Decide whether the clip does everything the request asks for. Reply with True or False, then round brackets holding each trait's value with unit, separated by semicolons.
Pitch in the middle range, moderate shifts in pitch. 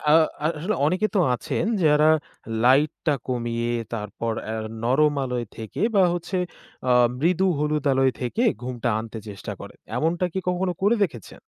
False (150 Hz; 6.5 semitones)